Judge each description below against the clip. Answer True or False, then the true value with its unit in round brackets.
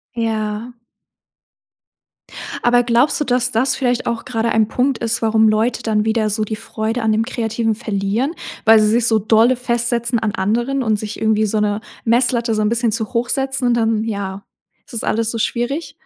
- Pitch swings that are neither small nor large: False (1.9 semitones)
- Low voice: False (225 Hz)